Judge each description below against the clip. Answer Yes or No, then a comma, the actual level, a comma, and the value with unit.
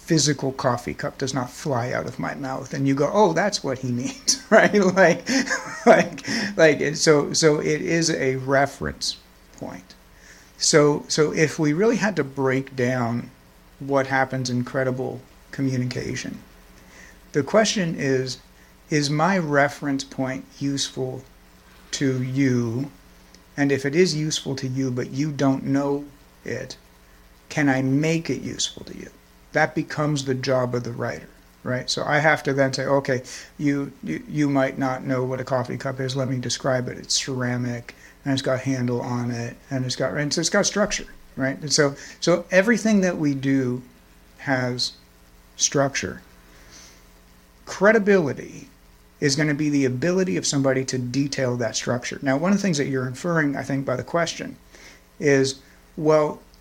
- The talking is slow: No, average, 165 wpm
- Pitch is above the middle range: No, low, 135 Hz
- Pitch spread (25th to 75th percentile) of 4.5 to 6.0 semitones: No, average, 3.4 semitones